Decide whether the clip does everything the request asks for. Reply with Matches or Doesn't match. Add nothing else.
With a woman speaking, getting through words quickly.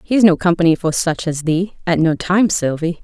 Matches